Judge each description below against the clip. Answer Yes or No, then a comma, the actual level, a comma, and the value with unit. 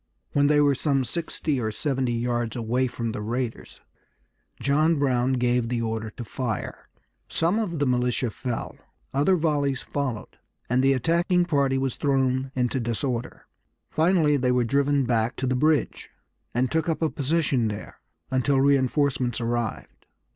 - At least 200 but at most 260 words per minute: No, average, 155 wpm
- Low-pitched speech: Yes, low, 130 Hz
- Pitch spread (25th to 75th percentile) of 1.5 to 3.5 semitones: Yes, average, 3.0 semitones